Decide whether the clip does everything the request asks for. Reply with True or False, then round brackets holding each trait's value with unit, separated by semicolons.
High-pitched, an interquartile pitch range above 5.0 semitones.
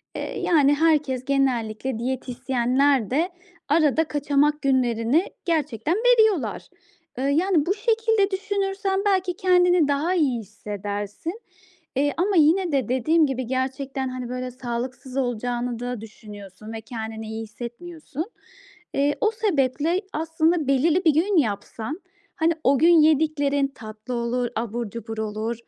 True (275 Hz; 5.5 semitones)